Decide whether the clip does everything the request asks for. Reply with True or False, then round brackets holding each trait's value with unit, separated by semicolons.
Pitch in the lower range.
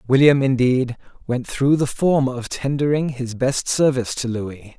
True (130 Hz)